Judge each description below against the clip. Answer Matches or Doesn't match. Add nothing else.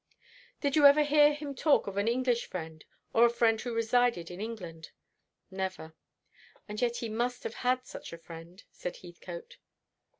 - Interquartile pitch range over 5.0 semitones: Matches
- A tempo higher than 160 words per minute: Matches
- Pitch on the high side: Matches